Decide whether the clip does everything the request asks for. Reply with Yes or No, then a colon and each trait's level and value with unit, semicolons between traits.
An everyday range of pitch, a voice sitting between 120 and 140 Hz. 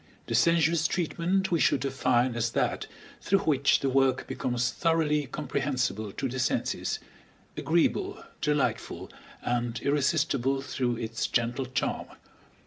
Yes: average, 3.8 semitones; low, 135 Hz